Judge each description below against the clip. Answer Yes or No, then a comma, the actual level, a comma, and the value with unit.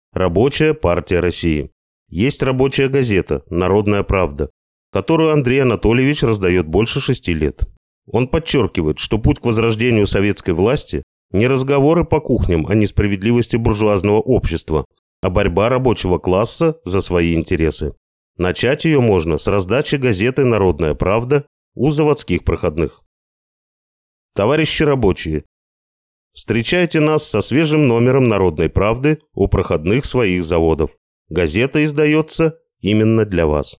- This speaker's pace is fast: No, average, 120 wpm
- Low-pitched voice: Yes, low, 110 Hz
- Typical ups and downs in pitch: No, wide, 7.4 semitones